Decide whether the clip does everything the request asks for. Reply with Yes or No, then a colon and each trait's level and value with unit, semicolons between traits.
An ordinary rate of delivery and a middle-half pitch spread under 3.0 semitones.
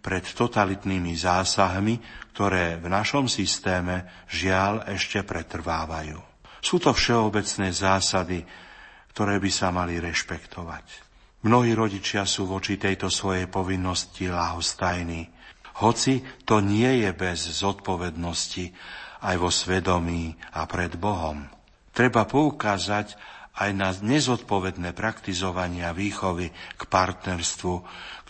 No: slow, 105 wpm; narrow, 2.6 semitones